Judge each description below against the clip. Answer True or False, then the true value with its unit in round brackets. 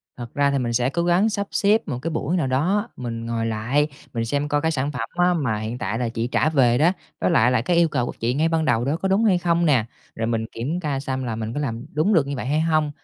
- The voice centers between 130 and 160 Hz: True (140 Hz)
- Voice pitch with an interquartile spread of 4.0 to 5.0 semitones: False (5.6 semitones)